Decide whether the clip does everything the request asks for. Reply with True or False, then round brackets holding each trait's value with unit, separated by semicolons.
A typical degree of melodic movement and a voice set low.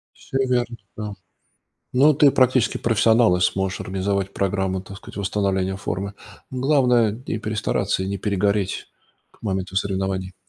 True (3.2 semitones; 100 Hz)